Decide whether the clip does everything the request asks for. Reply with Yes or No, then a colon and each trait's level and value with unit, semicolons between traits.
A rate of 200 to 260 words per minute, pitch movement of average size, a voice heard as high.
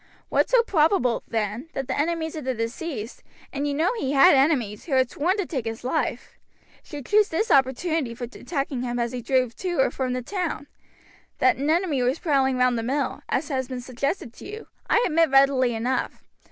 Yes: fast, 205 wpm; average, 4.5 semitones; very high, 270 Hz